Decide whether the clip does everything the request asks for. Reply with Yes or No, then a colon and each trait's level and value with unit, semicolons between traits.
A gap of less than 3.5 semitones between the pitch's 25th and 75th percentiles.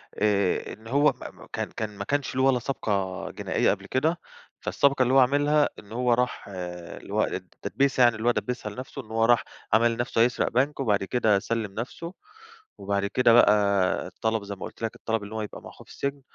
No: average, 3.8 semitones